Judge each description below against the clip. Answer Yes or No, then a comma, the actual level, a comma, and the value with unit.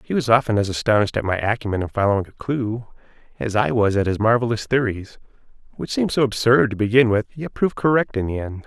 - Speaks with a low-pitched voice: Yes, low, 115 Hz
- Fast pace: Yes, fast, 220 wpm